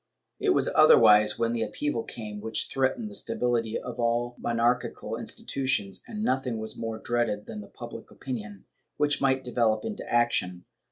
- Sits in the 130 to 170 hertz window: No, low, 120 Hz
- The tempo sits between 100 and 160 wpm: Yes, average, 155 wpm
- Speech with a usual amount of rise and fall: Yes, average, 3.0 semitones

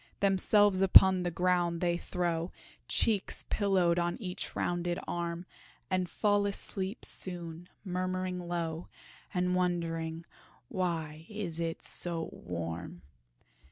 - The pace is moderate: No, slow, 110 wpm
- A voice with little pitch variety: Yes, narrow, 1.8 semitones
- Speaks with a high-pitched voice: No, medium, 175 Hz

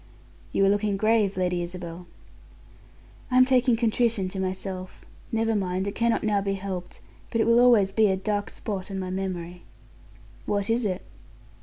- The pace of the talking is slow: No, average, 165 wpm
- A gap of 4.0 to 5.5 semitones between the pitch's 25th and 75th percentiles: No, average, 3.3 semitones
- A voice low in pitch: No, high, 200 Hz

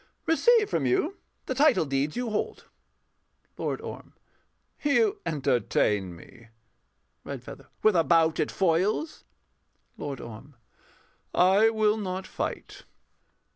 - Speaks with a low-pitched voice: No, medium, 185 Hz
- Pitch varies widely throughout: Yes, wide, 8.6 semitones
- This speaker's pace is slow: Yes, slow, 110 wpm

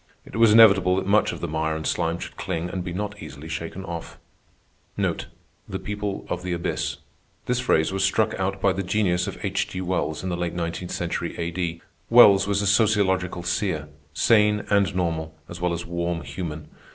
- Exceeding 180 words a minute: Yes, average, 190 wpm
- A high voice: No, very low, 90 Hz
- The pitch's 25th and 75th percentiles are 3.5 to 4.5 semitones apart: No, average, 2.8 semitones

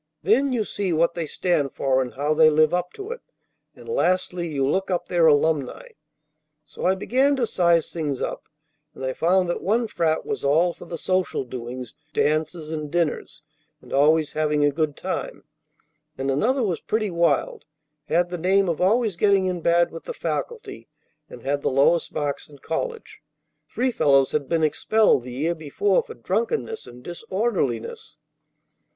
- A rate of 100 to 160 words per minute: No, average, 175 wpm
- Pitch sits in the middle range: Yes, medium, 170 Hz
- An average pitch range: Yes, average, 4.7 semitones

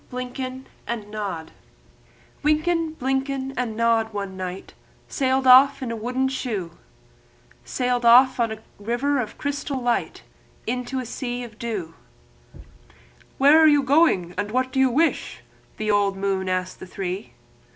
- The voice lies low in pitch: No, high, 245 Hz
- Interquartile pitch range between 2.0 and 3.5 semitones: No, average, 4.2 semitones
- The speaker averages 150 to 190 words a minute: No, average, 140 wpm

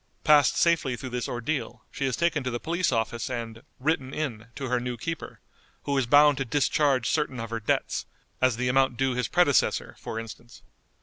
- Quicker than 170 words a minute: Yes, average, 195 wpm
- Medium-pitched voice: No, low, 130 Hz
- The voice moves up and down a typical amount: Yes, average, 3.5 semitones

